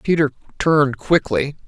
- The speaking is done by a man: Yes, male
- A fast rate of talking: No, slow, 110 wpm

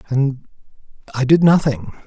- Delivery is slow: Yes, slow, 115 wpm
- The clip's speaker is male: Yes, male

